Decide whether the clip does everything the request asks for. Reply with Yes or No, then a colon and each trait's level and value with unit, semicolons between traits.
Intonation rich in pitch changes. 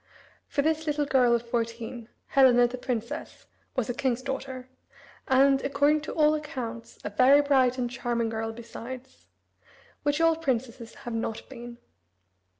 No: average, 2.9 semitones